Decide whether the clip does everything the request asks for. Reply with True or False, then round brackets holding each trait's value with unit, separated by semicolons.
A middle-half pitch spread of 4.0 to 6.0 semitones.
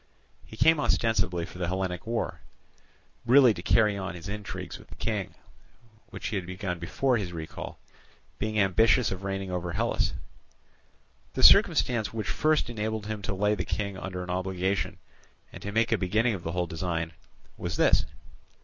False (3.4 semitones)